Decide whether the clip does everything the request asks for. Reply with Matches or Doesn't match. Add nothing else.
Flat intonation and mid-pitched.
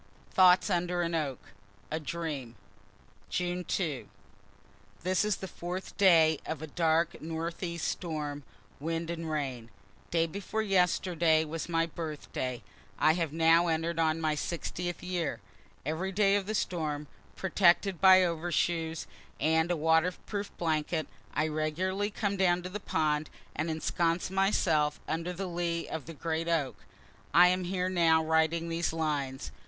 Matches